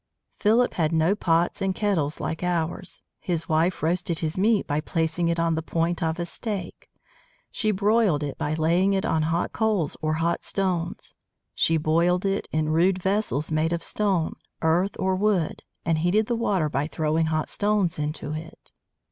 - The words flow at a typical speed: Yes, average, 175 wpm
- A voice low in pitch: No, medium, 170 Hz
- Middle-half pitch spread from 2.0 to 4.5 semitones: Yes, average, 3.3 semitones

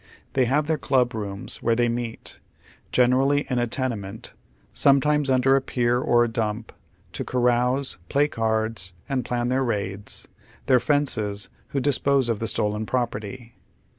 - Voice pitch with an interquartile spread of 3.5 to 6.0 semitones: No, average, 3.1 semitones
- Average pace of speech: Yes, average, 160 wpm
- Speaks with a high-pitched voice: No, low, 120 Hz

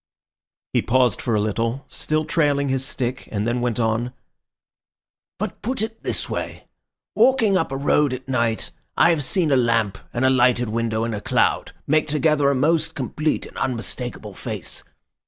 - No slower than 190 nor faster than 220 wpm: No, average, 175 wpm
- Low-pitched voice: Yes, low, 130 Hz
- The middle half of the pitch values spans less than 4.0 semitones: No, average, 4.5 semitones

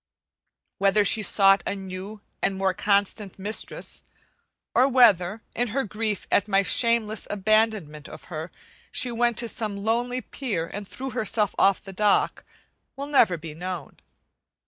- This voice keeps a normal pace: Yes, average, 145 wpm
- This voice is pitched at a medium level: No, high, 205 Hz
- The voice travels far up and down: No, average, 2.9 semitones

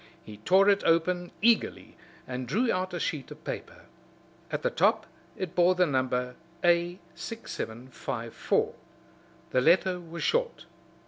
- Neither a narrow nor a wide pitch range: No, wide, 6.3 semitones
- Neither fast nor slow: No, slow, 130 wpm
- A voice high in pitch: No, medium, 175 Hz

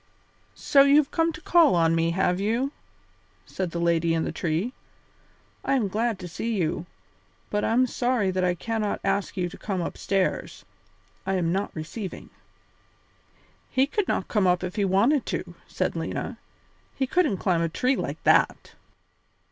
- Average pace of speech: Yes, average, 170 wpm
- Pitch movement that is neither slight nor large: No, wide, 6.1 semitones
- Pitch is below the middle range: No, high, 195 Hz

